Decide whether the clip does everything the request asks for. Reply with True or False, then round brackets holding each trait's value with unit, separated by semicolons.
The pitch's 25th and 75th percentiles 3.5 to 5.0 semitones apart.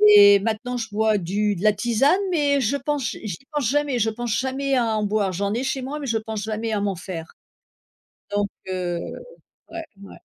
True (4.5 semitones)